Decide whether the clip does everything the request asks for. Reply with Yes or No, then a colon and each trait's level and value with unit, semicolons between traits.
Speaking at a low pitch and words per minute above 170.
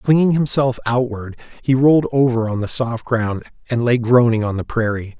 Yes: low, 120 Hz; average, 185 wpm